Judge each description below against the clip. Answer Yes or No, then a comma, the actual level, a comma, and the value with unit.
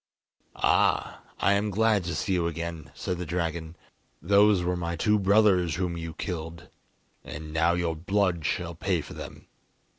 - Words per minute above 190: No, average, 160 wpm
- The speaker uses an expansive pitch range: No, average, 2.9 semitones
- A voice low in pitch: Yes, very low, 85 Hz